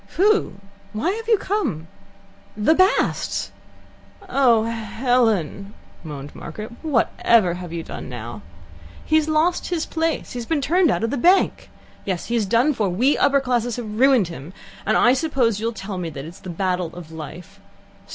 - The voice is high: Yes, high, 230 Hz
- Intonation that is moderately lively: No, wide, 8.2 semitones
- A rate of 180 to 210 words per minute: No, average, 165 wpm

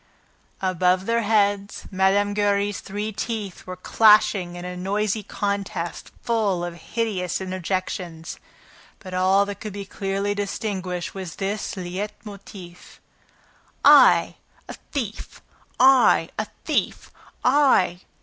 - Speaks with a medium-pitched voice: No, high, 200 Hz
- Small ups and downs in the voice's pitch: Yes, narrow, 2.3 semitones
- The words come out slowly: Yes, slow, 115 wpm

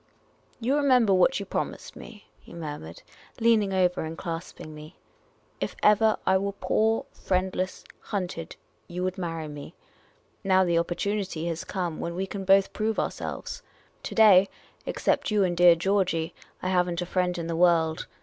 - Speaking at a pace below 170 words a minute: No, average, 185 wpm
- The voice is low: No, medium, 185 Hz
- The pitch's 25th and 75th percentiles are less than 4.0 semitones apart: Yes, average, 2.9 semitones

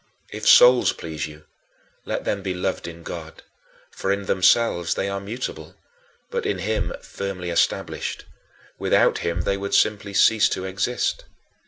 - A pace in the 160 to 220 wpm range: No, average, 150 wpm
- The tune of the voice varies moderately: Yes, average, 3.2 semitones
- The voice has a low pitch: Yes, low, 100 Hz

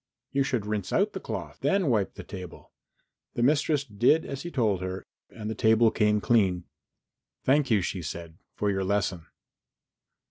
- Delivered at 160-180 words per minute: Yes, average, 170 wpm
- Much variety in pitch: Yes, wide, 5.9 semitones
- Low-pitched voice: Yes, low, 110 Hz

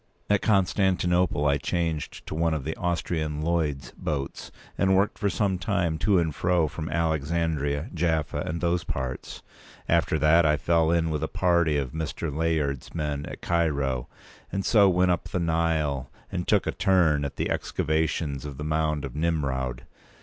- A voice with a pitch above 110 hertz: No, very low, 80 Hz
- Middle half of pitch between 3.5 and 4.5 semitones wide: No, average, 2.8 semitones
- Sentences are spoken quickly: No, average, 165 wpm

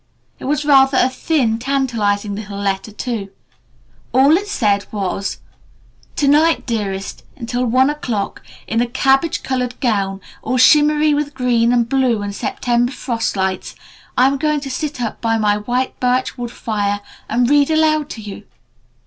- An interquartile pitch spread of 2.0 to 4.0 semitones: No, average, 4.7 semitones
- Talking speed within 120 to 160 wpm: Yes, average, 155 wpm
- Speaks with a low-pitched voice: No, high, 245 Hz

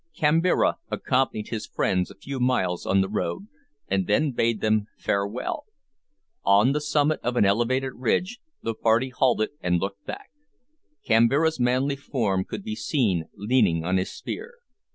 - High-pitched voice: No, low, 120 Hz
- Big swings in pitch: Yes, wide, 5.7 semitones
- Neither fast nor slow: Yes, average, 155 wpm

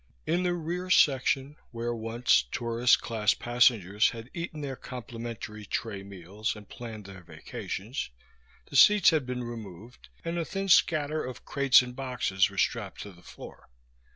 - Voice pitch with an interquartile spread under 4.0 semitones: No, average, 4.7 semitones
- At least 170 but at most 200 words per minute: No, average, 155 wpm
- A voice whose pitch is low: Yes, low, 120 Hz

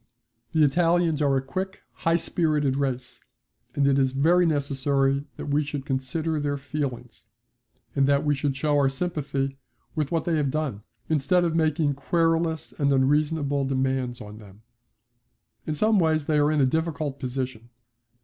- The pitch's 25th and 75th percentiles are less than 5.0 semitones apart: Yes, average, 2.8 semitones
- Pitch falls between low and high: Yes, medium, 145 Hz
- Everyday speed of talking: Yes, average, 160 wpm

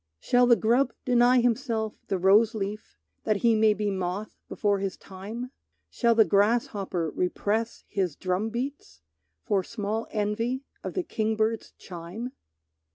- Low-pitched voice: No, high, 215 Hz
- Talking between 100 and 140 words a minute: Yes, slow, 135 wpm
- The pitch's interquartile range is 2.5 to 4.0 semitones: Yes, average, 3.0 semitones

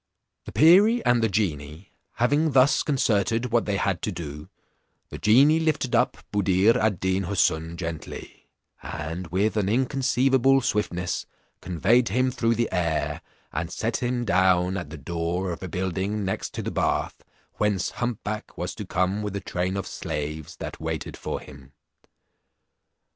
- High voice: No, low, 100 Hz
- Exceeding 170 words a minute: No, average, 160 wpm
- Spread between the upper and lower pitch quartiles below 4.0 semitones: No, wide, 5.5 semitones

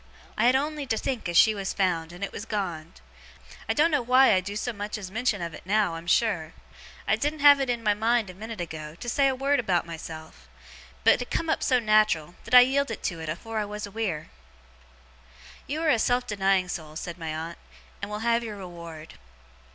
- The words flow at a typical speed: No, fast, 220 wpm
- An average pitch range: No, wide, 6.1 semitones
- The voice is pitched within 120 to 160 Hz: No, high, 210 Hz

